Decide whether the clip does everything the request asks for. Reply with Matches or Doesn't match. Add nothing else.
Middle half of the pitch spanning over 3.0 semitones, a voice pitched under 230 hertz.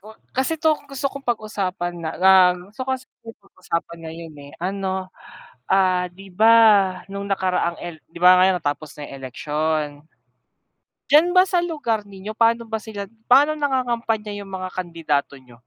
Matches